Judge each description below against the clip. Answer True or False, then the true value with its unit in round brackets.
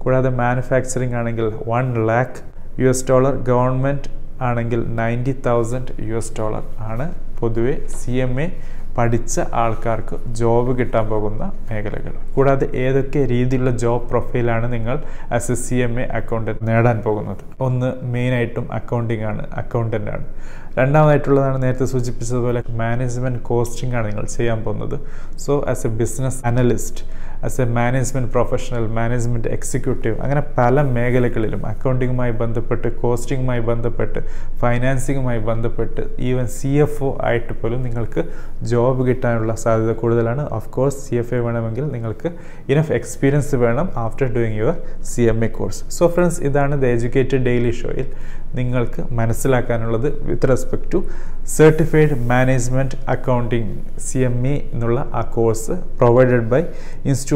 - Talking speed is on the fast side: True (130 wpm)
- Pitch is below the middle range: True (120 Hz)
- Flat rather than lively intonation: True (2.1 semitones)